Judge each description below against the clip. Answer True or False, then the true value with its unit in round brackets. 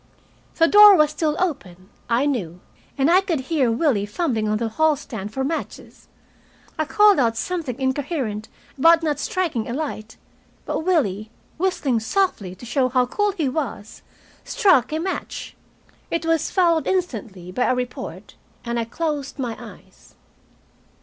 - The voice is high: True (275 Hz)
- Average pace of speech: True (155 wpm)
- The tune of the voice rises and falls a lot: True (6.3 semitones)